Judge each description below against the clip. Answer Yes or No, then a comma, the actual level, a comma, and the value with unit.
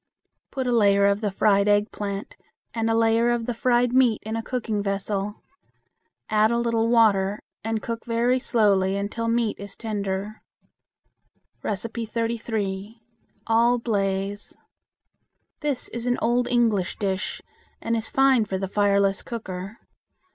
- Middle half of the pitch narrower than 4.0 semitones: Yes, average, 2.8 semitones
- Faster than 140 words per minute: No, slow, 135 wpm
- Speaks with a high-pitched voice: Yes, high, 220 Hz